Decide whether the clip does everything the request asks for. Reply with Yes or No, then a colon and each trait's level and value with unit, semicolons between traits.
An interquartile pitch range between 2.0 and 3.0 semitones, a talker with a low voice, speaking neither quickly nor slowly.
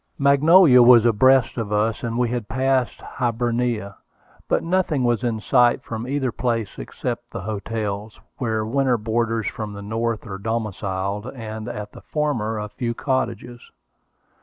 Yes: narrow, 2.6 semitones; low, 115 Hz; average, 150 wpm